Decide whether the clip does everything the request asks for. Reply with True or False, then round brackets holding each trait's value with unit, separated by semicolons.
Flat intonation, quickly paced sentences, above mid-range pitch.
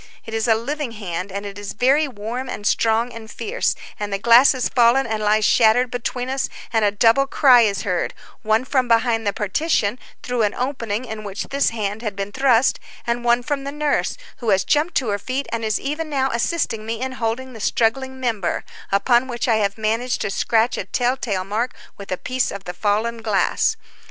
False (3.4 semitones; 210 wpm; 230 Hz)